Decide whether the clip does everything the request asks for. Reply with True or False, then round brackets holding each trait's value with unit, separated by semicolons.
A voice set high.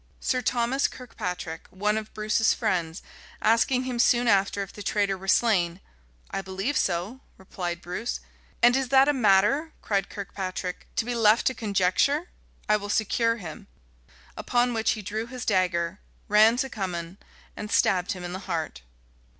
True (210 Hz)